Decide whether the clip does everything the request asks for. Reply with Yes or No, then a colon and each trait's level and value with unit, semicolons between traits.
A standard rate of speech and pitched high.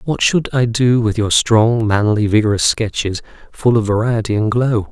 No: average, 185 wpm; low, 110 Hz